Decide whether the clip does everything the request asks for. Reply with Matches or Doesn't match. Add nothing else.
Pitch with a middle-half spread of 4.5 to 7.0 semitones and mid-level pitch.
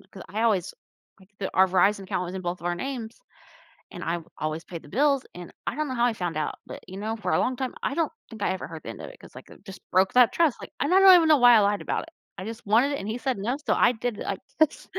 Doesn't match